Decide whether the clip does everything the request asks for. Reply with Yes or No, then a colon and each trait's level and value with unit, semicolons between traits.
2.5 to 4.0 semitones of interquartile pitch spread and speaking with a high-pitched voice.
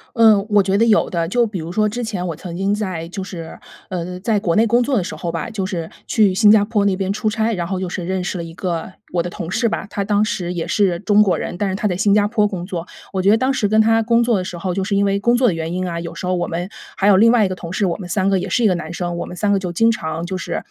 Yes: average, 3.2 semitones; high, 195 Hz